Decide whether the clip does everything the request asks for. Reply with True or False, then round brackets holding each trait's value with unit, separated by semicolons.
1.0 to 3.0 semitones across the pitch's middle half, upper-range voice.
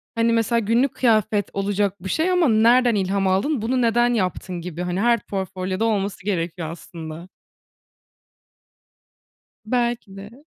False (4.1 semitones; 205 Hz)